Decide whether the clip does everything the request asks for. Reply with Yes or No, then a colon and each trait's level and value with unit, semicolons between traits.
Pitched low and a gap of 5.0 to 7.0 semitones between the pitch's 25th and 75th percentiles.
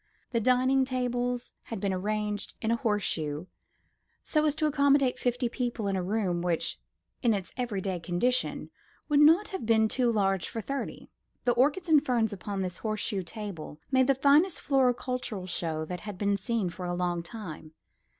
No: high, 225 Hz; average, 5.3 semitones